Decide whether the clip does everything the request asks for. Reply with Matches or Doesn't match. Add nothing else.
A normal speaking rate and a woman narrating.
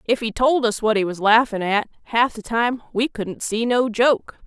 Doesn't match